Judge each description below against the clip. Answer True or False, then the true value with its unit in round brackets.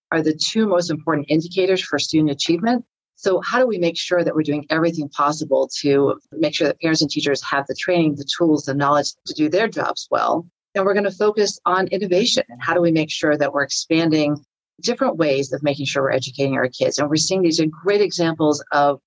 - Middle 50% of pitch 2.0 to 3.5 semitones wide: False (4.2 semitones)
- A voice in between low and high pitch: True (160 Hz)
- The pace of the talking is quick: True (225 wpm)